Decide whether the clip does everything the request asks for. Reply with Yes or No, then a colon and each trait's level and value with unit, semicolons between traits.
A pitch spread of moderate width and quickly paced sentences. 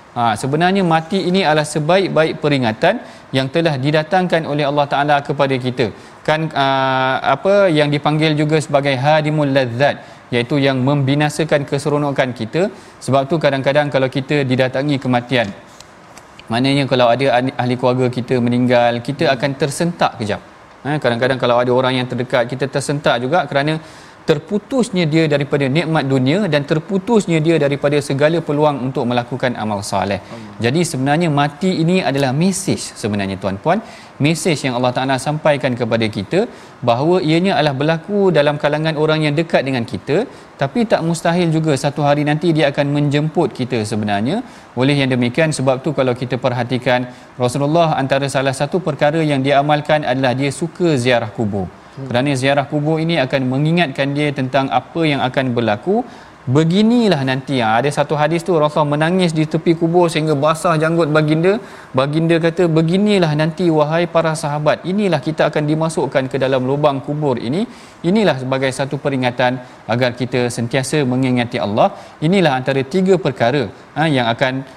Yes: average, 3.7 semitones; fast, 150 wpm